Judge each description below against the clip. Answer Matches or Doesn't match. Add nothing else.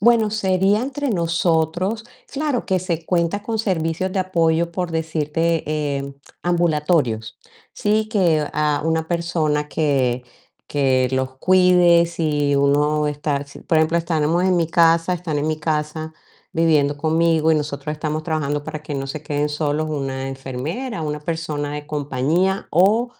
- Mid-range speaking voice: Matches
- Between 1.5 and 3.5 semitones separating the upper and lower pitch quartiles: Matches